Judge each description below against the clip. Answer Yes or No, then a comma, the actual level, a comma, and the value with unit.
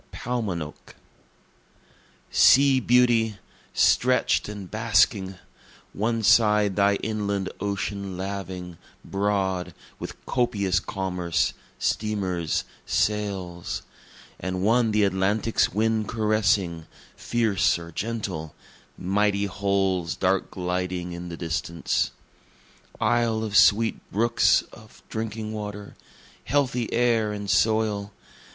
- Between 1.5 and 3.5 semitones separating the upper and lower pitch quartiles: Yes, average, 2.9 semitones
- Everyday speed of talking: No, slow, 95 wpm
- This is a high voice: No, low, 100 Hz